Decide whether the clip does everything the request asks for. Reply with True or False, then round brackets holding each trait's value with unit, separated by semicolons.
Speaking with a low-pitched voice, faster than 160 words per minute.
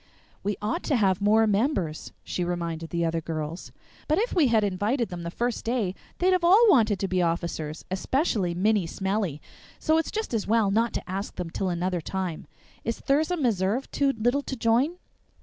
False (205 Hz; 190 wpm)